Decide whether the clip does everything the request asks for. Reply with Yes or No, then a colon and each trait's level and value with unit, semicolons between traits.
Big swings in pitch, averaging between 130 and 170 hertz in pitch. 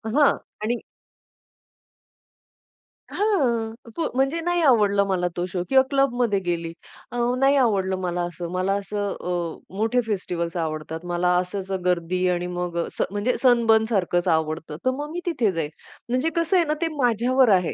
No: wide, 6.3 semitones; high, 200 Hz